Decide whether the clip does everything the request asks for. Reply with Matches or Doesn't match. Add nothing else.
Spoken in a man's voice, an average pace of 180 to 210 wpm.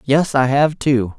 Matches